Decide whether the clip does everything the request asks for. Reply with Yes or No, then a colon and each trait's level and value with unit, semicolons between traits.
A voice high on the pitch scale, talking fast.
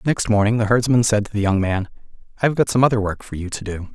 No: low, 110 Hz; fast, 290 wpm